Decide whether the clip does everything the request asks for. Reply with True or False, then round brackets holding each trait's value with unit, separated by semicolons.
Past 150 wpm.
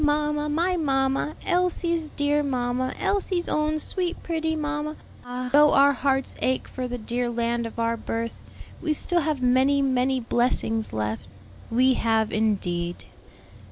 False (145 wpm)